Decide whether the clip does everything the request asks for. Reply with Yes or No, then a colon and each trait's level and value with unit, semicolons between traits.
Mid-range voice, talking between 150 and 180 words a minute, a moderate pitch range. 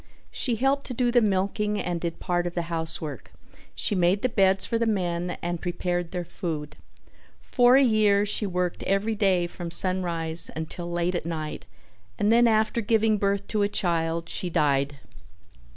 Yes: medium, 180 Hz; average, 175 wpm; average, 3.7 semitones